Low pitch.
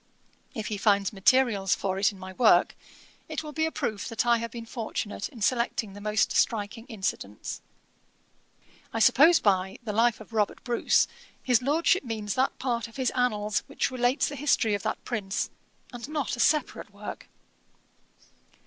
No: high, 230 Hz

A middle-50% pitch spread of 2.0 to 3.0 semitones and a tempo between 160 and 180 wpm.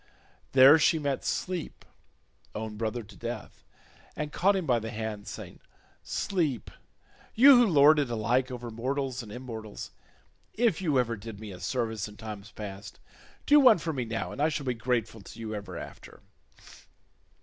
No: average, 5.2 semitones; average, 170 wpm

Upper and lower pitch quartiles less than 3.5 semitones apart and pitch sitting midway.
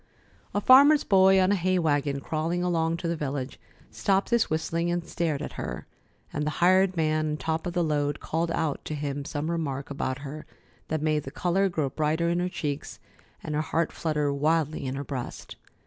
Yes: average, 3.0 semitones; medium, 160 Hz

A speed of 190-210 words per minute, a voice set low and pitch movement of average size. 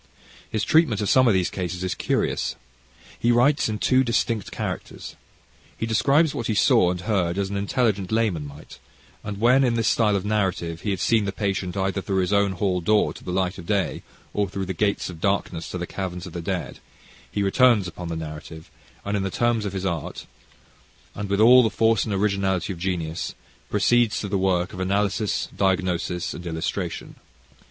Yes: average, 200 wpm; low, 100 Hz; average, 3.0 semitones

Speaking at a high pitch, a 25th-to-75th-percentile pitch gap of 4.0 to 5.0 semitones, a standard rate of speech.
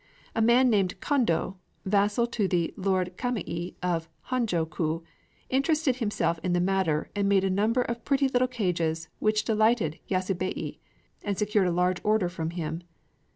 Yes: high, 195 Hz; average, 4.7 semitones; average, 155 wpm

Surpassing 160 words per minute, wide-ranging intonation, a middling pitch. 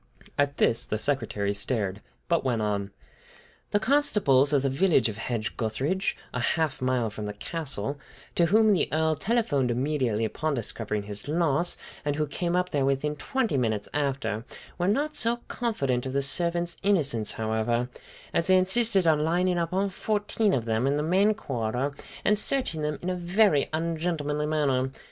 Yes: average, 175 wpm; wide, 6.6 semitones; medium, 145 Hz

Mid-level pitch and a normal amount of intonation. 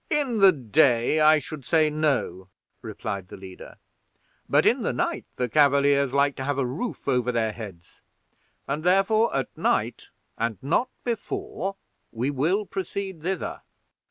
No: medium, 145 Hz; wide, 7.1 semitones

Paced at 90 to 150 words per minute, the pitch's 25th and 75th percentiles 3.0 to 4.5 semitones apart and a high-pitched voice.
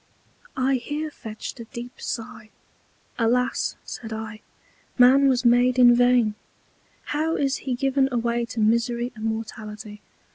No: slow, 135 wpm; narrow, 2.4 semitones; high, 240 Hz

